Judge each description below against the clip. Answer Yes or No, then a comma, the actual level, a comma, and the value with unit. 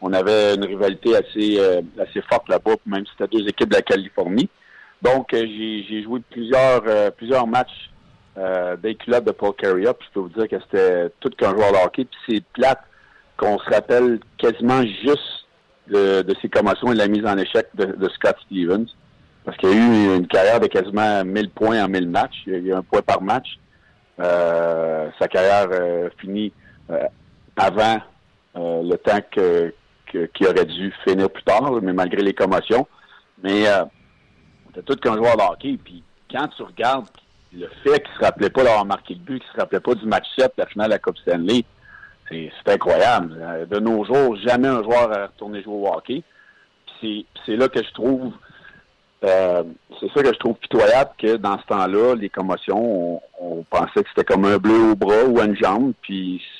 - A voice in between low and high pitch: No, low, 105 Hz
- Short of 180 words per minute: No, average, 210 wpm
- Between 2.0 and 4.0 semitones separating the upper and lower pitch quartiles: Yes, average, 3.6 semitones